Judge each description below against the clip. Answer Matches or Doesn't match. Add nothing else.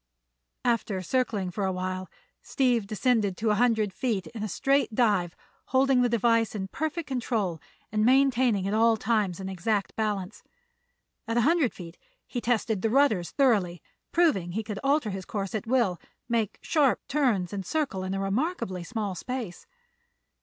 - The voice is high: Matches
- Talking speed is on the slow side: Doesn't match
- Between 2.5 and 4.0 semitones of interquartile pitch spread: Doesn't match